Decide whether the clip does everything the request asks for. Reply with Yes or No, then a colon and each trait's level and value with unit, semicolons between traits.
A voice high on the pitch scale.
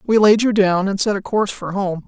Yes: high, 200 Hz